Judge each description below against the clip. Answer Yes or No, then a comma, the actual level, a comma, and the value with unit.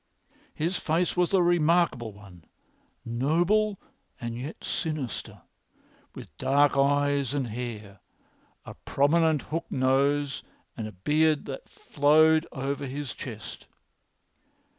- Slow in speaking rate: Yes, slow, 110 wpm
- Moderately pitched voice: Yes, medium, 145 Hz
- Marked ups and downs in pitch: No, average, 3.7 semitones